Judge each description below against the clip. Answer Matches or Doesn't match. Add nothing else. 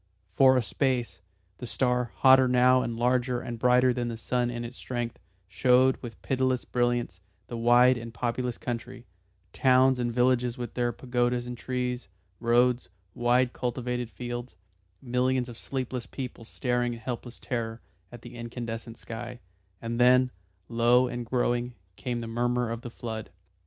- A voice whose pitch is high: Doesn't match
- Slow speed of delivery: Doesn't match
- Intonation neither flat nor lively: Doesn't match